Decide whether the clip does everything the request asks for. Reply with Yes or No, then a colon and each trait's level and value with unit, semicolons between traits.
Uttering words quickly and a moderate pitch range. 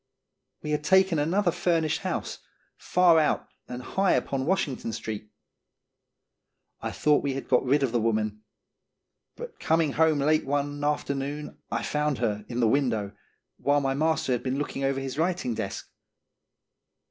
No: average, 160 wpm; average, 4.0 semitones